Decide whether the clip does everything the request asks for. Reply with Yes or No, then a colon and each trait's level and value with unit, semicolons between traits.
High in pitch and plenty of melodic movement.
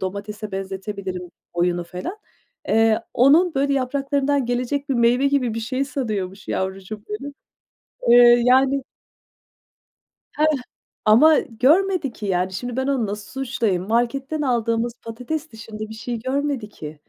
No: high, 235 Hz; average, 4.6 semitones